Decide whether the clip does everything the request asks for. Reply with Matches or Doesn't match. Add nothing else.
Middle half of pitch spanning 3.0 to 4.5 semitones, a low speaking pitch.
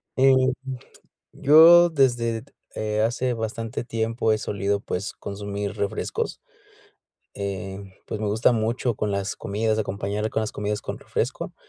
Doesn't match